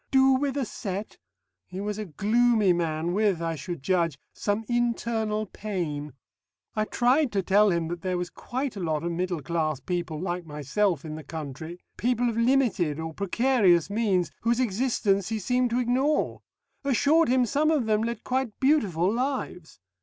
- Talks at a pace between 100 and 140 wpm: No, average, 170 wpm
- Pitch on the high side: Yes, high, 205 Hz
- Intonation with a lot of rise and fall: Yes, wide, 6.1 semitones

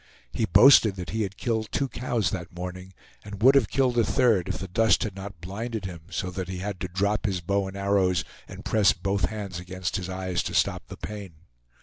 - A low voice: Yes, low, 100 Hz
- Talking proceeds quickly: Yes, fast, 225 wpm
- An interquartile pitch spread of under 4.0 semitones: Yes, average, 2.9 semitones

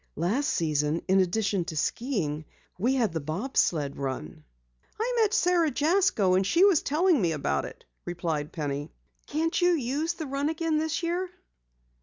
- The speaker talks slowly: No, average, 165 wpm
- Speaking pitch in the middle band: No, high, 235 Hz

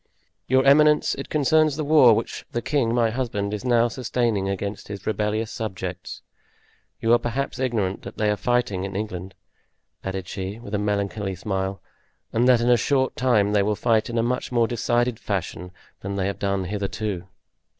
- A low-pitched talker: Yes, low, 110 Hz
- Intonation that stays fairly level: No, average, 3.7 semitones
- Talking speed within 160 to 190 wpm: Yes, average, 180 wpm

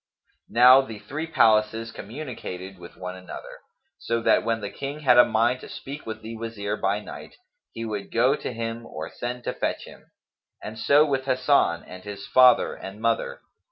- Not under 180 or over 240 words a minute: Yes, average, 185 wpm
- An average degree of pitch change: Yes, average, 3.5 semitones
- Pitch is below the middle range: Yes, low, 115 Hz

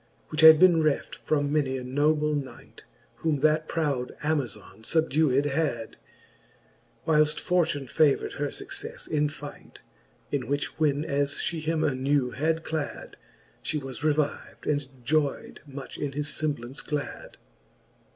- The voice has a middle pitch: Yes, medium, 145 Hz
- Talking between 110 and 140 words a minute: Yes, slow, 135 wpm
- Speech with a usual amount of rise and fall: No, narrow, 2.0 semitones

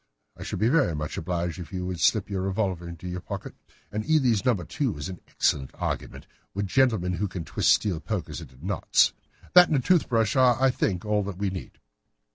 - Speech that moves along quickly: Yes, fast, 215 wpm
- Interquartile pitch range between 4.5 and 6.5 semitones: Yes, average, 4.8 semitones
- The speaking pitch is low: Yes, very low, 95 Hz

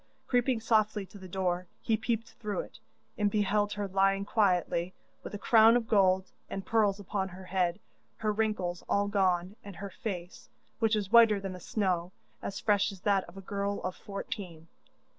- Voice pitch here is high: Yes, high, 200 Hz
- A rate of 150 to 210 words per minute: Yes, average, 180 wpm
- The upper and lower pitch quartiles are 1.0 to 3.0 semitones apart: Yes, narrow, 2.4 semitones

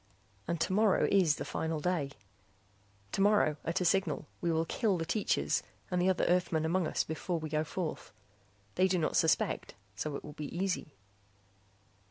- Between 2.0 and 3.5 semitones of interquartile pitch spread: Yes, average, 3.1 semitones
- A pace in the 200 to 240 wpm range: No, average, 170 wpm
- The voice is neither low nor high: Yes, medium, 170 Hz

